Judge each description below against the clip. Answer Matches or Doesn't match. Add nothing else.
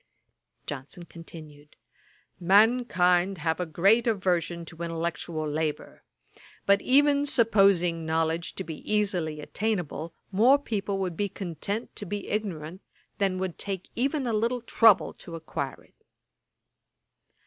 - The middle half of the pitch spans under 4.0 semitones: Doesn't match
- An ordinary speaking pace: Doesn't match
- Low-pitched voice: Doesn't match